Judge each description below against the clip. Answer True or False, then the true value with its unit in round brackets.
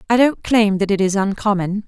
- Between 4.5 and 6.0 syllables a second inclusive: True (5.4 syllables/s)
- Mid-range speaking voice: False (205 Hz)